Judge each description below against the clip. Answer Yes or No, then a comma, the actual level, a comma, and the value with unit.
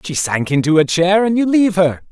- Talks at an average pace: No, fast, 255 wpm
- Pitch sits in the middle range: Yes, medium, 175 Hz